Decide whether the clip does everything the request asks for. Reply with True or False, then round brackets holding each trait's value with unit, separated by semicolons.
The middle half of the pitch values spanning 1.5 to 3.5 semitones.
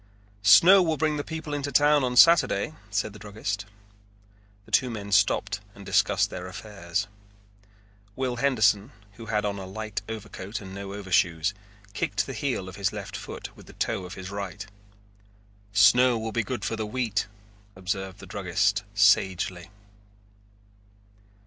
False (4.0 semitones)